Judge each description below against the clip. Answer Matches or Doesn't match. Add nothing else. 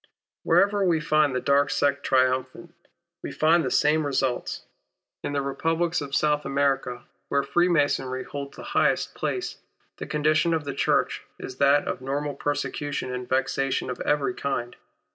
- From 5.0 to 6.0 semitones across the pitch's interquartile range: Doesn't match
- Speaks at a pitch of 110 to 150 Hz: Matches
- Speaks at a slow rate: Doesn't match